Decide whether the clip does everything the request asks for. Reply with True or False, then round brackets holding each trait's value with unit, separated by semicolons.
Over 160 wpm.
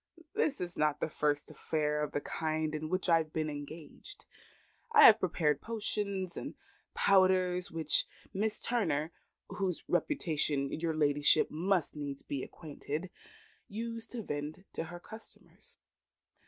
False (140 wpm)